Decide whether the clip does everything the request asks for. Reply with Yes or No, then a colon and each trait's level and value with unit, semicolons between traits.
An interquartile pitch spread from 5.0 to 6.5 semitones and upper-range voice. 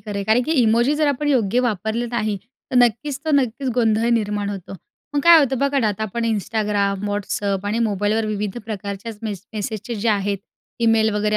No: narrow, 2.6 semitones; high, 220 Hz